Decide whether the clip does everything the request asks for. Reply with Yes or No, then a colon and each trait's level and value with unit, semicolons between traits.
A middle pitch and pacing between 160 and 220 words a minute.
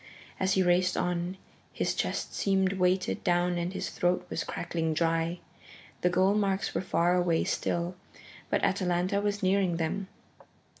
No: medium, 180 Hz; average, 150 wpm